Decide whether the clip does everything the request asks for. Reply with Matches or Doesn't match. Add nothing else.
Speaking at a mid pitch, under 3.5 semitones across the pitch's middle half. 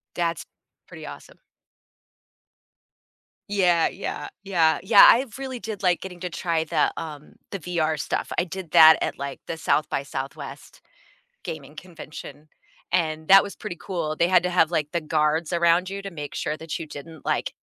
Matches